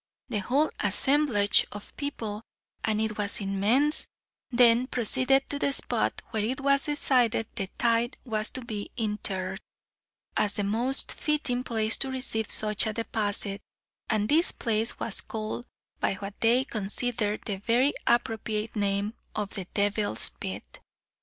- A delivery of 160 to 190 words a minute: No, average, 145 wpm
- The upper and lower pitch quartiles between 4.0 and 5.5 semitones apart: No, average, 3.4 semitones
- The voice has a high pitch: Yes, high, 220 Hz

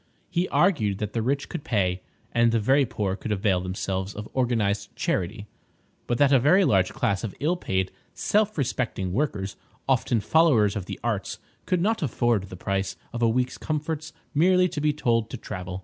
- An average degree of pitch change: No, wide, 6.8 semitones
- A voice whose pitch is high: No, low, 115 Hz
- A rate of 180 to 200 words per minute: Yes, average, 185 wpm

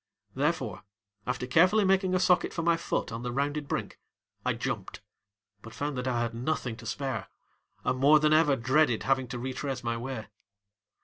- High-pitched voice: No, low, 135 Hz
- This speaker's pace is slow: No, average, 180 wpm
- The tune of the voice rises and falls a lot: No, average, 4.2 semitones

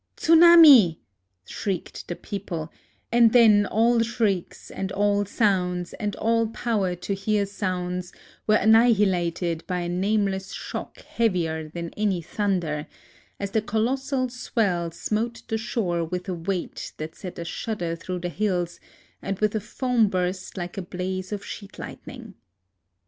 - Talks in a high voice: Yes, high, 195 Hz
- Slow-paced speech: No, average, 155 wpm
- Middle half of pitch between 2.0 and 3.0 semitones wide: No, average, 3.7 semitones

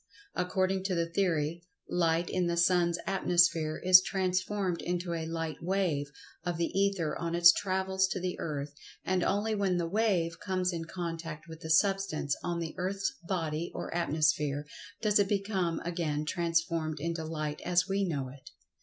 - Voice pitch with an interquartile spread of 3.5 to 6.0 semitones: No, narrow, 2.6 semitones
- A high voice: No, medium, 170 Hz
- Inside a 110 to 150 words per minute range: No, average, 170 wpm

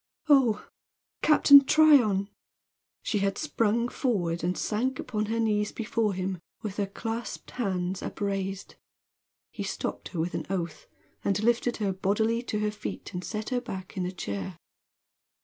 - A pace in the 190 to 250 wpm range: No, average, 150 wpm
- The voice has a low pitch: No, high, 210 Hz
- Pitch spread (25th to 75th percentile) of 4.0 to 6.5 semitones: No, average, 3.6 semitones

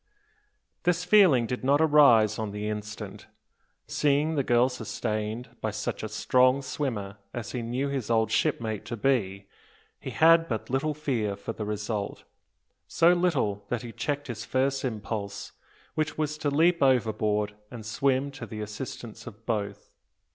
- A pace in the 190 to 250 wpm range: No, average, 155 wpm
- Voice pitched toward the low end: Yes, low, 120 Hz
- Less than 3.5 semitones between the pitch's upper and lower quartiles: No, average, 4.6 semitones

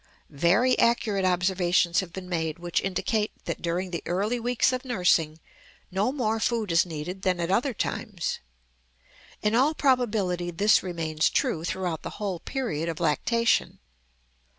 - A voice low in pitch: No, medium, 185 Hz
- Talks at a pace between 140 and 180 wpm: Yes, average, 150 wpm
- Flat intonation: No, average, 4.9 semitones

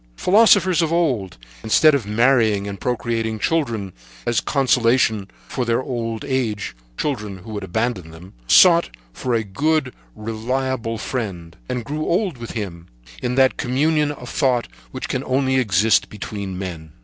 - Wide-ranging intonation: No, average, 4.4 semitones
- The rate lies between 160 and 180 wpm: No, average, 150 wpm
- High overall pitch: No, low, 120 Hz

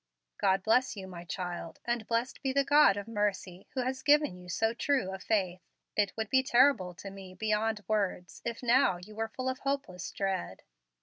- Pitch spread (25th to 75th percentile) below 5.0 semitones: No, average, 5.3 semitones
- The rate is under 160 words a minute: No, average, 195 wpm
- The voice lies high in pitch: Yes, high, 215 Hz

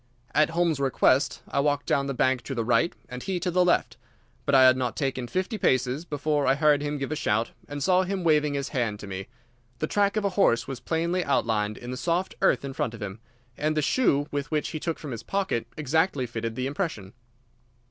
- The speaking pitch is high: No, medium, 145 Hz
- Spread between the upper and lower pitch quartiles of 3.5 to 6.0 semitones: Yes, average, 4.6 semitones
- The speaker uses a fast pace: Yes, fast, 225 wpm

